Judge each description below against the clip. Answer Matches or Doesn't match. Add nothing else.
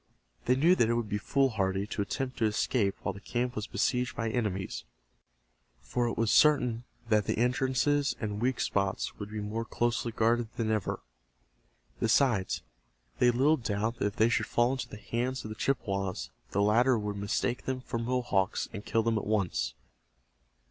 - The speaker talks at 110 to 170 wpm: Doesn't match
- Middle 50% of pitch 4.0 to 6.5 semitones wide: Doesn't match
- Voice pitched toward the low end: Matches